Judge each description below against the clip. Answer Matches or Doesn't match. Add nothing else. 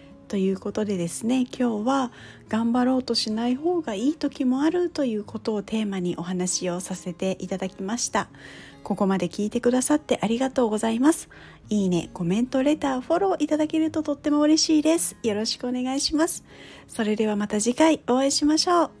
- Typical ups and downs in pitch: Doesn't match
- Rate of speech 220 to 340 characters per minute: Doesn't match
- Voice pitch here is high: Matches